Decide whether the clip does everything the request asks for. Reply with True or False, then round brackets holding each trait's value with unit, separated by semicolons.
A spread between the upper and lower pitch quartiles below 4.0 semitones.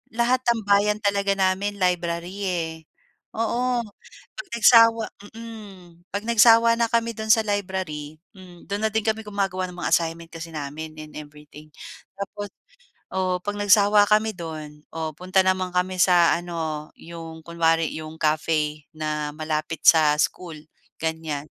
False (4.3 semitones)